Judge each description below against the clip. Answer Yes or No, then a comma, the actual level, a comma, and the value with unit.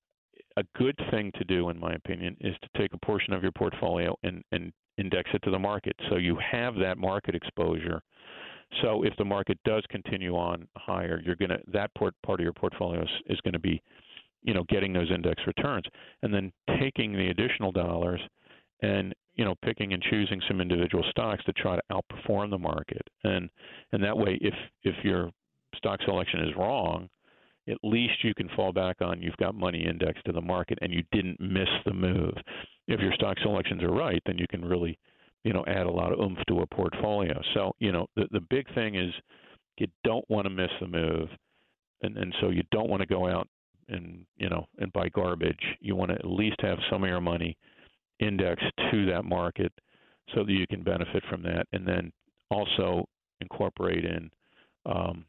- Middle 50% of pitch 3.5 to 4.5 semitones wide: No, average, 3.0 semitones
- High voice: No, very low, 95 Hz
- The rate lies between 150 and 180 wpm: No, average, 200 wpm